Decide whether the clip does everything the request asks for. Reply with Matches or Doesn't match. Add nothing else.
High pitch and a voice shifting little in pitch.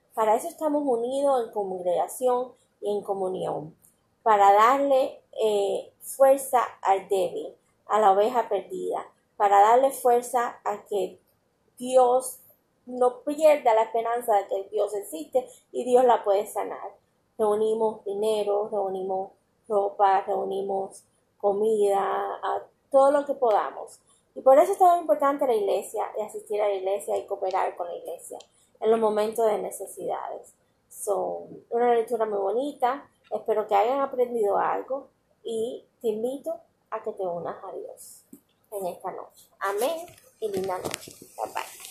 Doesn't match